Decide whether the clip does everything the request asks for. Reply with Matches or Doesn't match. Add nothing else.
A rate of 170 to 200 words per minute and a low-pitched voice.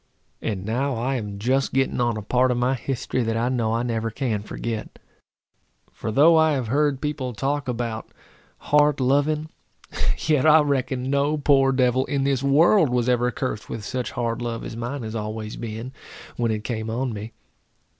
Matches